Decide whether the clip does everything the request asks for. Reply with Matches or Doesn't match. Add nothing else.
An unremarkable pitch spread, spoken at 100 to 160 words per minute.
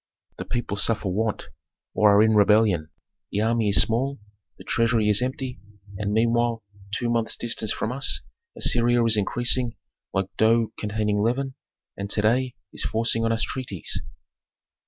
Doesn't match